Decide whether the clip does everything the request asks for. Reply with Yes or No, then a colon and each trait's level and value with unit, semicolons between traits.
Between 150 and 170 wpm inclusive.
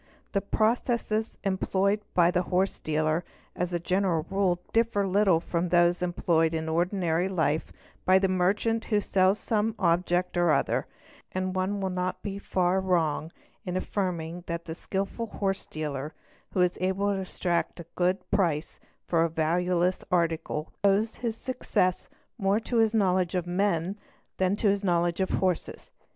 Yes: average, 160 wpm